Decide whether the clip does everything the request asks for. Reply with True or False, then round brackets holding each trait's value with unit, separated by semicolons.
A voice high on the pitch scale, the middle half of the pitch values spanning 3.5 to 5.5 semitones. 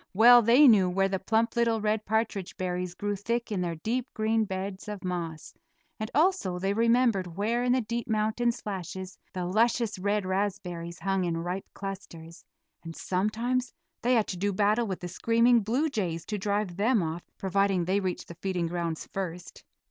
True (200 Hz; 3.9 semitones)